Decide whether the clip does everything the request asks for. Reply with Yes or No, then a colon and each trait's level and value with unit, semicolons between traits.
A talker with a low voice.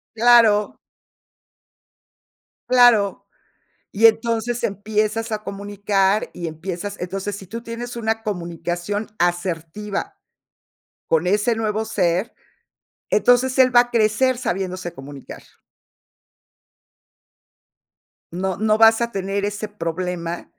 No: high, 205 Hz